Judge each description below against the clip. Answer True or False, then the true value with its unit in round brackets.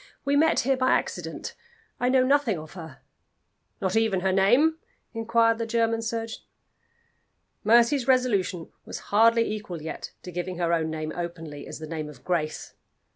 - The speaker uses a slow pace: False (160 wpm)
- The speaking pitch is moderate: False (215 Hz)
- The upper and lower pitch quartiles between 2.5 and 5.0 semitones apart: False (5.6 semitones)